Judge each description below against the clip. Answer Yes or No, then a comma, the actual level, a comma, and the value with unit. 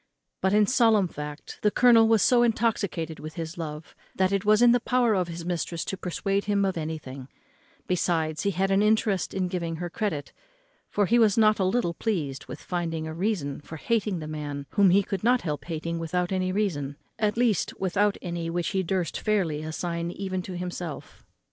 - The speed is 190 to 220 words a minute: Yes, average, 200 wpm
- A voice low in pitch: No, medium, 185 Hz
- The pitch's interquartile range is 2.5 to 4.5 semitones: Yes, average, 4.2 semitones